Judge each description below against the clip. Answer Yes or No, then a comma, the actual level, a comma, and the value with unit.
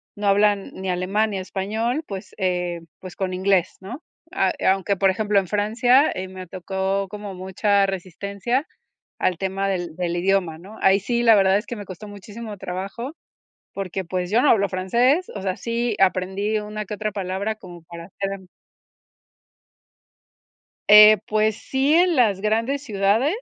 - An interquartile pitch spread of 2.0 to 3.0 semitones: Yes, narrow, 2.4 semitones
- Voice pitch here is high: Yes, high, 195 Hz